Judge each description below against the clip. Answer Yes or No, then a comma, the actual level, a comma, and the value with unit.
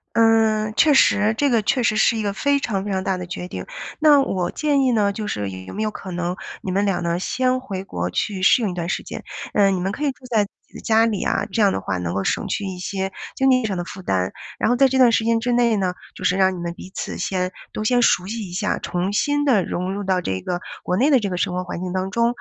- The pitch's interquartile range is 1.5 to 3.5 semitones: No, average, 4.2 semitones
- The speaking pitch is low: No, high, 200 Hz